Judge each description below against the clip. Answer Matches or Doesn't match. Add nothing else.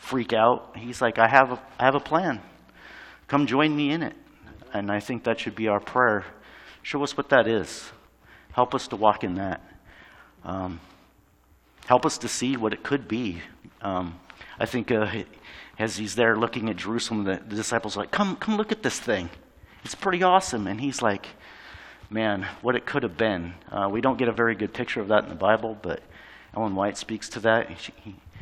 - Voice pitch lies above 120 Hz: Doesn't match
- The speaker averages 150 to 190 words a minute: Doesn't match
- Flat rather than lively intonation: Doesn't match